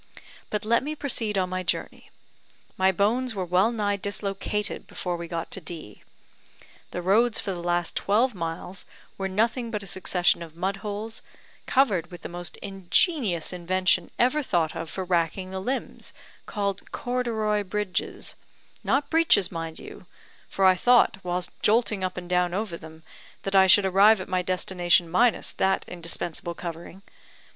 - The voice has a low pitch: No, high, 190 Hz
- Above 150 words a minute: Yes, average, 160 wpm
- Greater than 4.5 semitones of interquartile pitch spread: No, average, 3.3 semitones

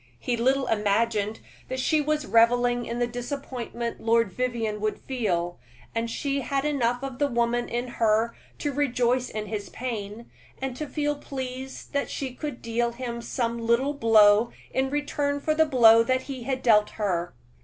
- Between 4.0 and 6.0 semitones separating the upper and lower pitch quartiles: No, average, 2.8 semitones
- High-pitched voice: Yes, high, 240 Hz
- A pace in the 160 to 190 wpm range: Yes, average, 165 wpm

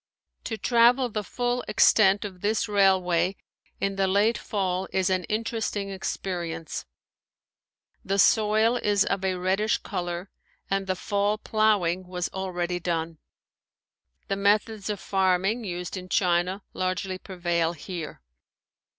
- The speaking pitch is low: No, high, 195 Hz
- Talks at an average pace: No, slow, 125 wpm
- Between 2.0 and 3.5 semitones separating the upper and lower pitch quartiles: Yes, average, 2.7 semitones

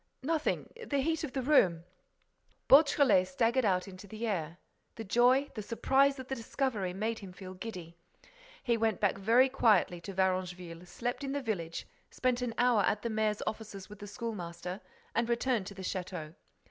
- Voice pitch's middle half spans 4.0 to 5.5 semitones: Yes, average, 5.2 semitones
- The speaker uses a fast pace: No, average, 175 wpm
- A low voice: No, high, 215 Hz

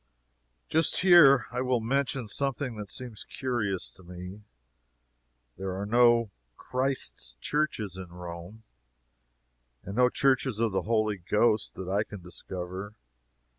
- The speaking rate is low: Yes, slow, 130 wpm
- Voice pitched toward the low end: Yes, low, 110 Hz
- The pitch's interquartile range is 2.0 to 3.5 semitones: No, average, 5.1 semitones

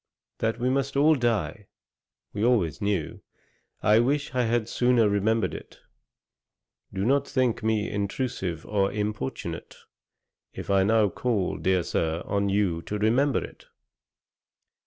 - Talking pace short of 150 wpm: Yes, slow, 135 wpm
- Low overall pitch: Yes, low, 110 Hz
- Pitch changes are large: No, average, 3.8 semitones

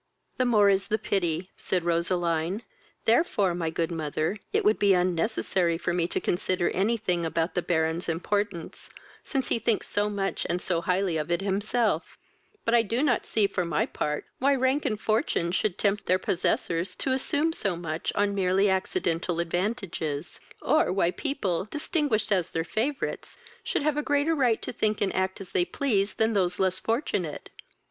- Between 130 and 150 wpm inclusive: No, average, 180 wpm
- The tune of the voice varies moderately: Yes, average, 4.4 semitones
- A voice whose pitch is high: Yes, high, 195 Hz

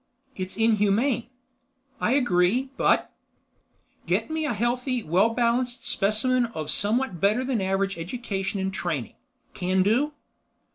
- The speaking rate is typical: No, slow, 125 wpm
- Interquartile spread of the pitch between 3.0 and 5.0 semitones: Yes, average, 4.7 semitones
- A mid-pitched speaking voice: No, high, 215 Hz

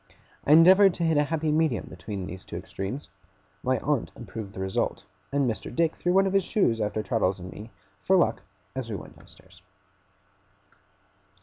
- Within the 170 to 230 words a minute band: Yes, average, 180 wpm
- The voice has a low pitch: Yes, low, 130 Hz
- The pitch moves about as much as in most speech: No, wide, 7.7 semitones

